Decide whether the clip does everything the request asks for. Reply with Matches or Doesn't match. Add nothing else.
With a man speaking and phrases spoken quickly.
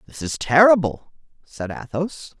Doesn't match